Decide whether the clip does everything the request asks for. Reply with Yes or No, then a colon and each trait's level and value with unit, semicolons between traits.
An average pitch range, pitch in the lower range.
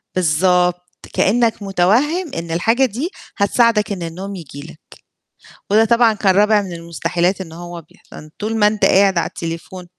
No: average, 4.0 semitones; high, 190 Hz